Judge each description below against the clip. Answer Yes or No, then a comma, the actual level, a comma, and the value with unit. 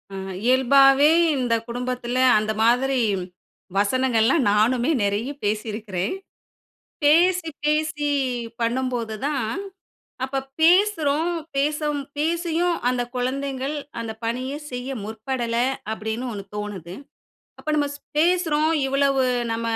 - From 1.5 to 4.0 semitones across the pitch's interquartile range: No, average, 4.5 semitones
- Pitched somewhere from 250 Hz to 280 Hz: Yes, very high, 260 Hz